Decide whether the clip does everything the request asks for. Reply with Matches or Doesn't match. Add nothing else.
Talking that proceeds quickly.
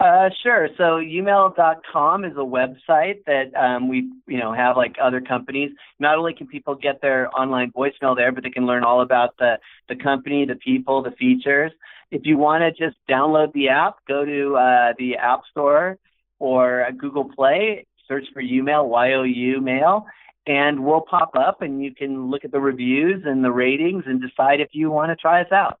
Doesn't match